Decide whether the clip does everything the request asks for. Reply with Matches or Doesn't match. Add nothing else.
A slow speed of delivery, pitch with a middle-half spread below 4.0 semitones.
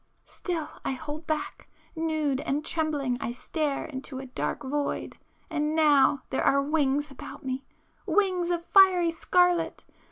Matches